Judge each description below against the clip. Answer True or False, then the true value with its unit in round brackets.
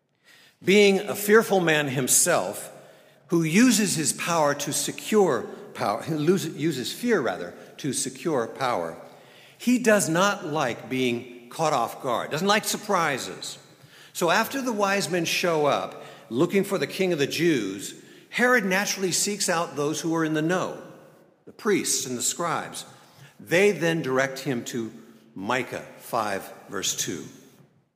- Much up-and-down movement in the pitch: True (5.7 semitones)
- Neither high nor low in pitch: True (170 Hz)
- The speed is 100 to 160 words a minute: True (145 wpm)